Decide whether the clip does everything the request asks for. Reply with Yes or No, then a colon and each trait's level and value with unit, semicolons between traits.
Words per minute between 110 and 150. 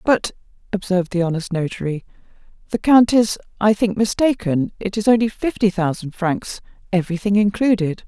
Yes: average, 140 wpm